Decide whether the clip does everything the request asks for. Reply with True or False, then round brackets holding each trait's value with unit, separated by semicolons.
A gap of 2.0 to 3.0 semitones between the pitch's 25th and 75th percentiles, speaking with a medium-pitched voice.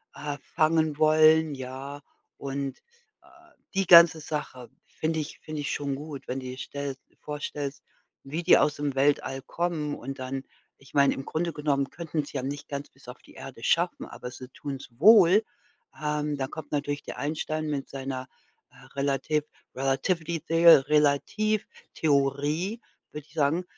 True (2.4 semitones; 145 Hz)